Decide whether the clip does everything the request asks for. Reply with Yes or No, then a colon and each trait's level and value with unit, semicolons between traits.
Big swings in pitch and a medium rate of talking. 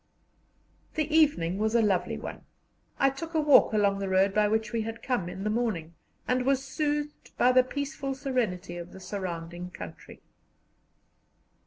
Yes: wide, 6.4 semitones; average, 165 wpm